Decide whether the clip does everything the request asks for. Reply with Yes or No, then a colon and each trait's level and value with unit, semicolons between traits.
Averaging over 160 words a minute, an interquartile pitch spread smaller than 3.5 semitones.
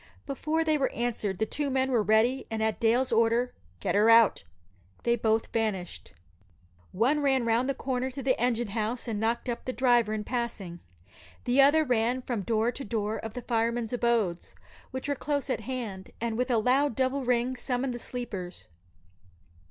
Yes: average, 185 wpm; average, 2.7 semitones